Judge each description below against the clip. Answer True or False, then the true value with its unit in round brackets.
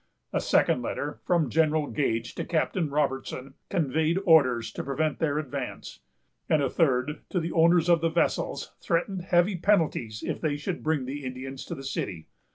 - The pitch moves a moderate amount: True (3.9 semitones)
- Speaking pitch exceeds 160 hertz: False (150 Hz)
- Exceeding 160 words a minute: True (170 wpm)